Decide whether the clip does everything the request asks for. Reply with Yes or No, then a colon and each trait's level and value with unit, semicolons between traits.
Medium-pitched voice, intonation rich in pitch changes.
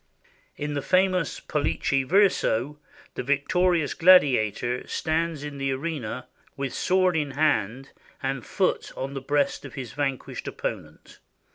No: medium, 145 Hz; average, 3.7 semitones